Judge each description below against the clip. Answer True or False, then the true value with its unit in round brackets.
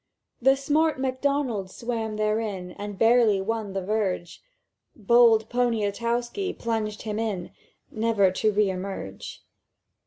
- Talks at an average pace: False (115 wpm)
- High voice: True (220 Hz)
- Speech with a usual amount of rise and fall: True (3.0 semitones)